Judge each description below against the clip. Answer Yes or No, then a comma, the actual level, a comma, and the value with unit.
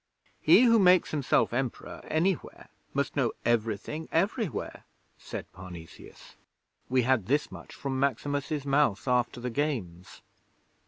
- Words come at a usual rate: No, slow, 120 wpm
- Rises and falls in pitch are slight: No, average, 4.7 semitones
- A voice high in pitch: No, low, 135 Hz